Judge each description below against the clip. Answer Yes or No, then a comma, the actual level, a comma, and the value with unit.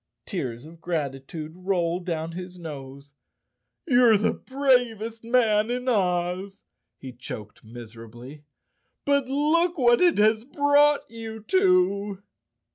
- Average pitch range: No, wide, 8.0 semitones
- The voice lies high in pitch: Yes, high, 200 Hz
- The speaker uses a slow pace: Yes, slow, 115 wpm